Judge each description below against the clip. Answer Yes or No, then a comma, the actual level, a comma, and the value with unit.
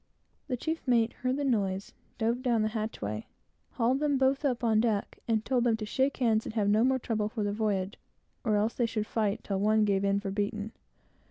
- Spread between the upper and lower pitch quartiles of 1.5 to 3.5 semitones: Yes, average, 3.0 semitones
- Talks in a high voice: Yes, high, 220 Hz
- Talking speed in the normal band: No, fast, 220 wpm